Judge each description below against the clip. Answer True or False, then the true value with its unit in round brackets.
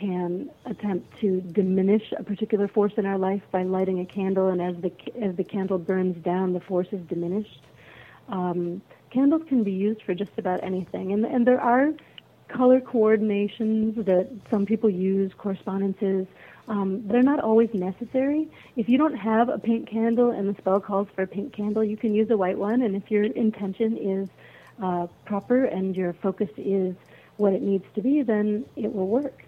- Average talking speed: True (185 wpm)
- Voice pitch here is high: True (205 Hz)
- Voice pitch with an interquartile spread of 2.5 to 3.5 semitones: True (2.9 semitones)